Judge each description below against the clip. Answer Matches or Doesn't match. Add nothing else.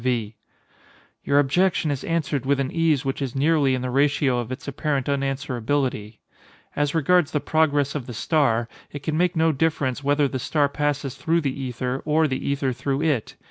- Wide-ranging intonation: Doesn't match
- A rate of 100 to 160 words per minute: Doesn't match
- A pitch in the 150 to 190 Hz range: Doesn't match